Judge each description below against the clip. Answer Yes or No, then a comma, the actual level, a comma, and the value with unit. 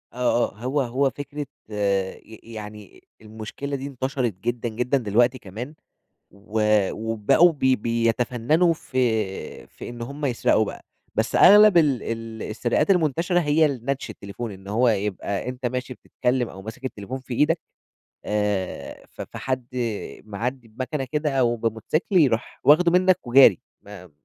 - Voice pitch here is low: Yes, low, 120 Hz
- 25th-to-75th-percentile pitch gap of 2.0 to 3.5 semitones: No, average, 4.1 semitones